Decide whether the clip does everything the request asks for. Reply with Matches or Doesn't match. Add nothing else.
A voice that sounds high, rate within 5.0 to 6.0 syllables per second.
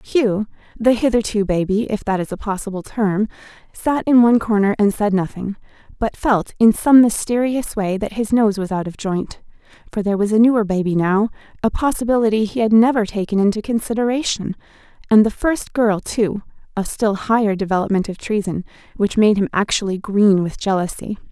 Matches